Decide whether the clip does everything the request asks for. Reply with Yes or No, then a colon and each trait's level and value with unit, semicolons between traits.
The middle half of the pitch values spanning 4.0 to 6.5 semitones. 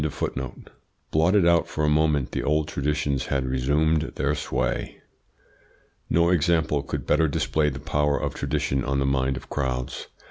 No: narrow, 2.5 semitones